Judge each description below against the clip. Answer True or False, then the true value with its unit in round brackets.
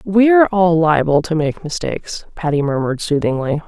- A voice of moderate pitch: True (165 Hz)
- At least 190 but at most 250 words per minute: False (145 wpm)